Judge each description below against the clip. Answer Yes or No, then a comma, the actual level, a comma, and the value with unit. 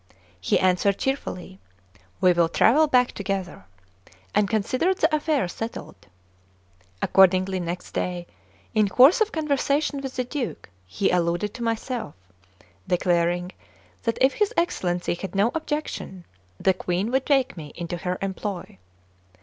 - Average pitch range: No, wide, 7.1 semitones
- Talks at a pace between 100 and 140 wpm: Yes, slow, 135 wpm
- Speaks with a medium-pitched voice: No, high, 200 Hz